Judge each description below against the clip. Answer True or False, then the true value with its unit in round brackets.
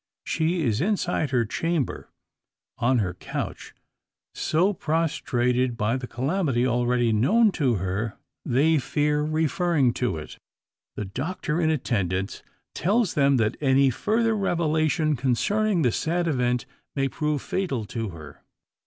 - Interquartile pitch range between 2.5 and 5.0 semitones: False (5.5 semitones)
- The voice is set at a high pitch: False (140 Hz)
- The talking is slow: True (130 wpm)